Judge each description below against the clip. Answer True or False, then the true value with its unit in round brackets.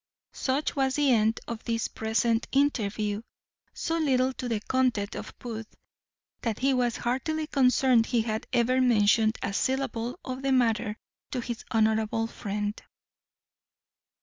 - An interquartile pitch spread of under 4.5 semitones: True (2.9 semitones)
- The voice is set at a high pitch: True (235 Hz)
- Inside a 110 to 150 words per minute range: True (140 wpm)